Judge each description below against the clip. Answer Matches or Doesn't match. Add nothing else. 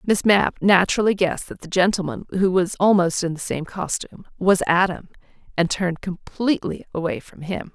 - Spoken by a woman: Matches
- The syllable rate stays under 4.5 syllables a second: Doesn't match